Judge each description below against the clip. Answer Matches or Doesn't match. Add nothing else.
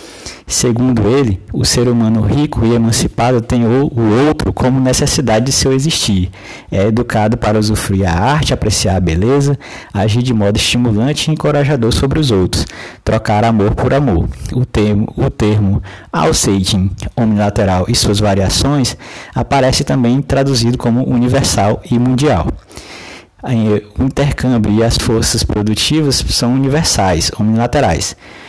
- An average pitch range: Matches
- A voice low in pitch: Matches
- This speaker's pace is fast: Doesn't match